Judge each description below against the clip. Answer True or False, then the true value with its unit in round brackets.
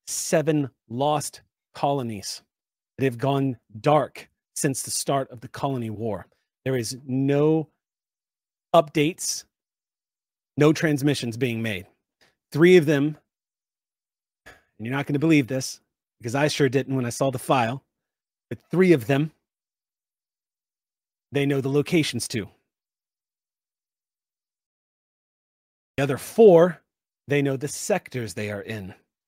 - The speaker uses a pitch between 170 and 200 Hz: False (140 Hz)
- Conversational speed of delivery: False (125 wpm)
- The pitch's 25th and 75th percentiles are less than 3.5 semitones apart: False (4.2 semitones)